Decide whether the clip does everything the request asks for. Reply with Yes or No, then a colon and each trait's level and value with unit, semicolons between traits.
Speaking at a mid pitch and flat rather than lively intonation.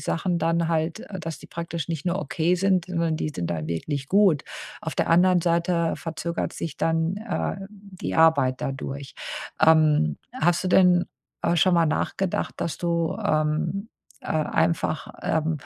Yes: medium, 165 Hz; narrow, 2.3 semitones